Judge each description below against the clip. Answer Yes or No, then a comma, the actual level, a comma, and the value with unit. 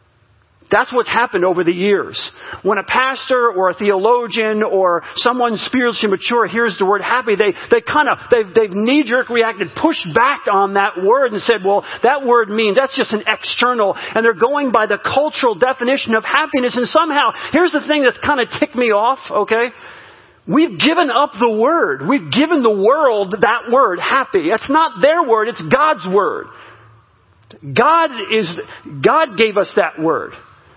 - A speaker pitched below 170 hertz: No, high, 235 Hz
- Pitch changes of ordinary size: No, wide, 5.7 semitones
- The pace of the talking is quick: No, average, 175 wpm